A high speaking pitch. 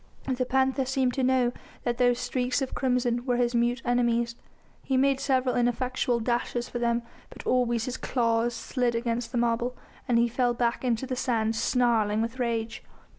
Yes: high, 245 Hz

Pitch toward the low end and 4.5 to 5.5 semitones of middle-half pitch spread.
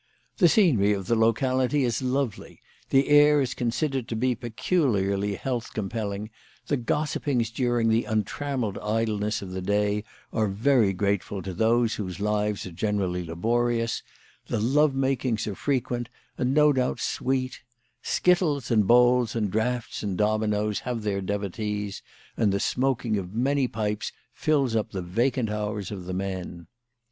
No: low, 115 Hz; average, 3.8 semitones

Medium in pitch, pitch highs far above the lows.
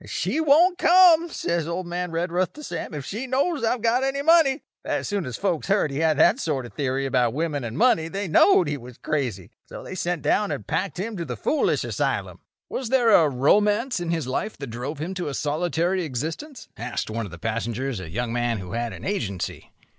Yes: medium, 165 Hz; wide, 9.0 semitones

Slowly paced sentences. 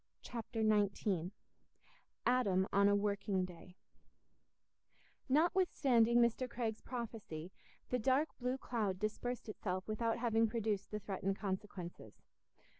Yes: slow, 110 wpm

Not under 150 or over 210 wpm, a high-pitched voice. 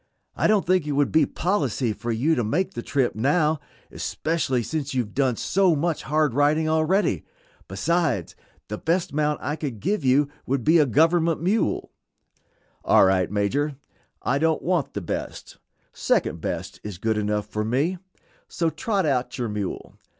No: average, 170 wpm; medium, 145 Hz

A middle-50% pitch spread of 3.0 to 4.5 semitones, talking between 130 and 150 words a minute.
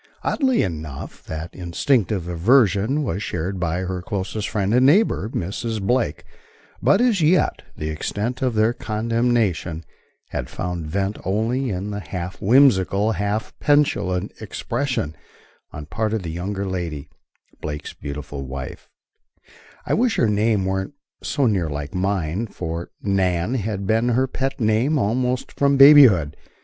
No: wide, 5.6 semitones; average, 140 wpm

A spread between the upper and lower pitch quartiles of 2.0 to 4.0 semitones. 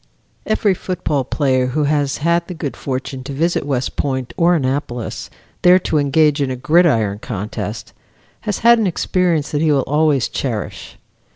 No: average, 4.6 semitones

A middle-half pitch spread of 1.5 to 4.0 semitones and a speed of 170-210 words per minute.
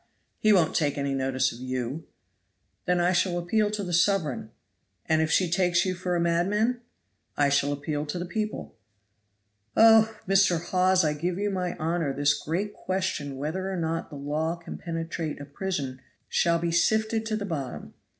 No: average, 4.4 semitones; average, 180 wpm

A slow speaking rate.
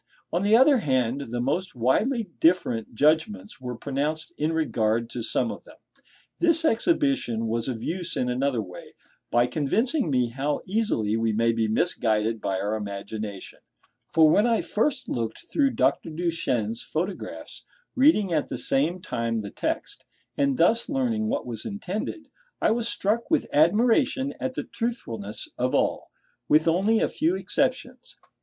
No: average, 155 wpm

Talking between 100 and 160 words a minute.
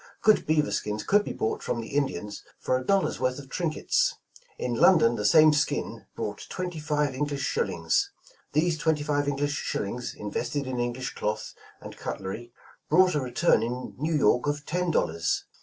No: average, 175 wpm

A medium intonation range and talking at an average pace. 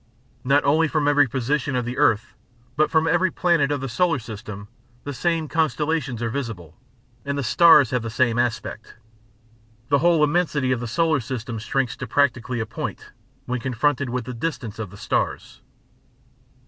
Yes: average, 4.1 semitones; average, 175 wpm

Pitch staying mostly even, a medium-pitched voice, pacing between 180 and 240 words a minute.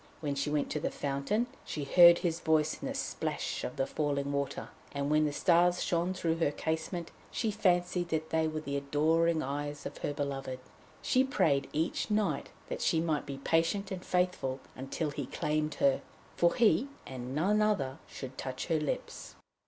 No: average, 3.6 semitones; medium, 155 Hz; average, 185 wpm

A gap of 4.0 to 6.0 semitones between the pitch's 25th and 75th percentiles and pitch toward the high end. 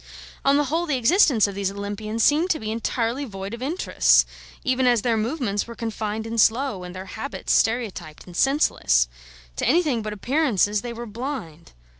Yes: average, 4.8 semitones; high, 230 Hz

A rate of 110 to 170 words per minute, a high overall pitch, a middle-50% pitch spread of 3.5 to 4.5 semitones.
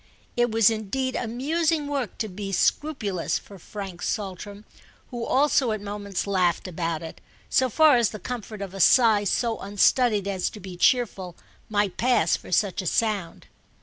Yes: average, 165 wpm; high, 210 Hz; average, 3.9 semitones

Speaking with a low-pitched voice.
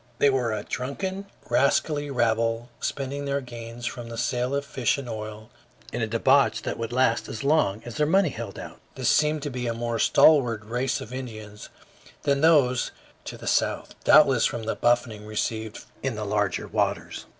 Yes: low, 120 Hz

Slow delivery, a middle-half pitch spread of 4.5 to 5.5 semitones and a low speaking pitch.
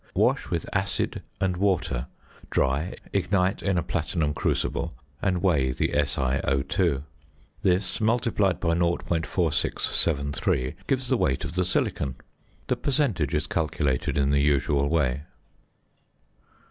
Yes: slow, 120 wpm; average, 4.9 semitones; very low, 80 Hz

